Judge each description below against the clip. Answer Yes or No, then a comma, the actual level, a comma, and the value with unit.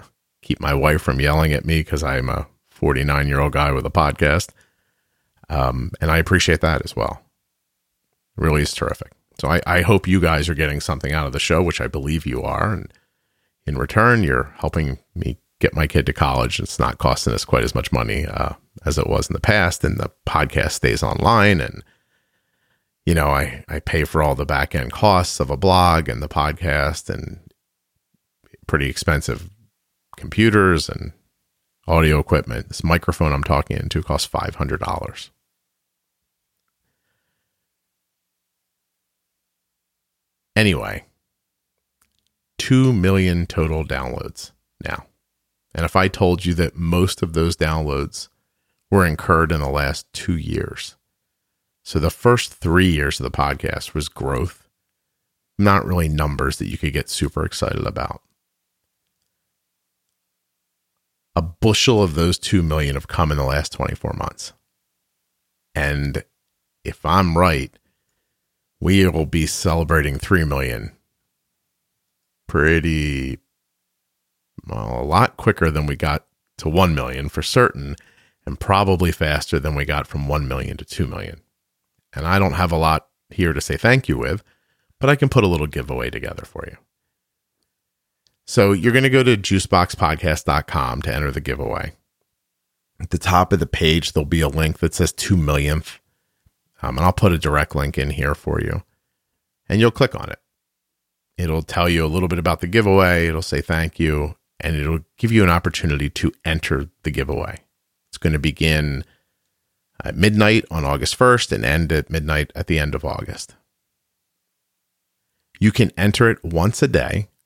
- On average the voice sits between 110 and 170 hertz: No, very low, 80 Hz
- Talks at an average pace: Yes, average, 160 wpm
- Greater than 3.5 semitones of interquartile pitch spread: Yes, average, 4.1 semitones